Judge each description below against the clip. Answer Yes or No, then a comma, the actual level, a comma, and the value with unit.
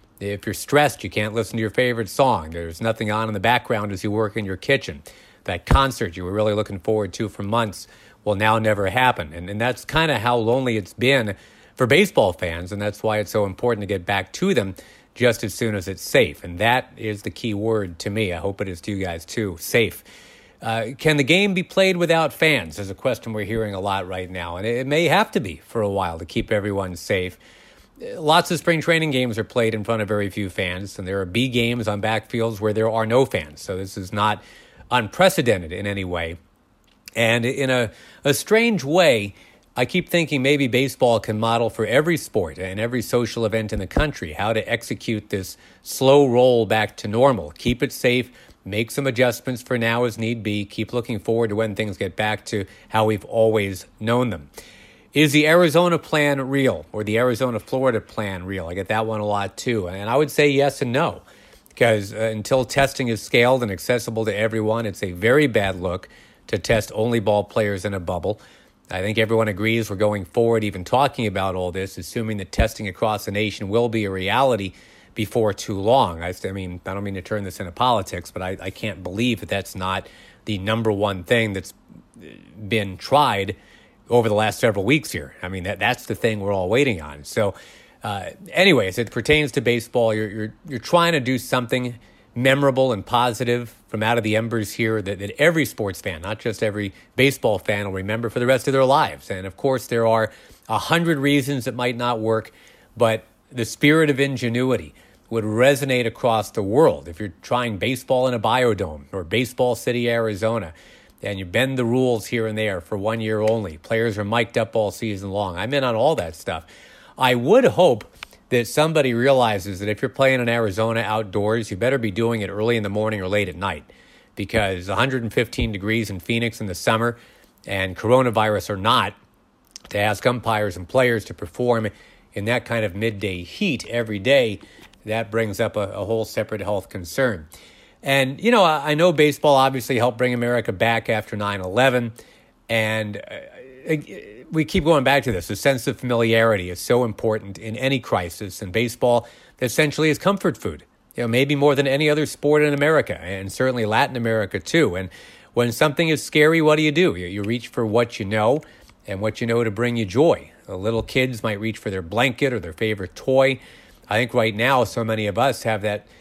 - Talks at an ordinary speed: No, fast, 210 wpm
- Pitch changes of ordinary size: Yes, average, 3.5 semitones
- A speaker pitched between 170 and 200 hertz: No, low, 110 Hz